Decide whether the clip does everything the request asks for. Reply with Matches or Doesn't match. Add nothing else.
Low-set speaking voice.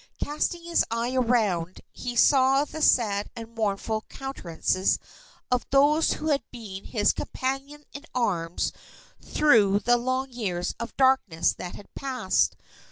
Doesn't match